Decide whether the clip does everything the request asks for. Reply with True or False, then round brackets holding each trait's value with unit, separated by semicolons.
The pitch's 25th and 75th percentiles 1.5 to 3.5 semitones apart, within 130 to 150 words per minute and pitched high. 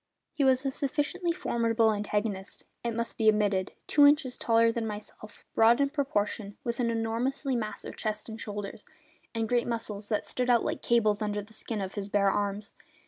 False (3.0 semitones; 185 wpm; 225 Hz)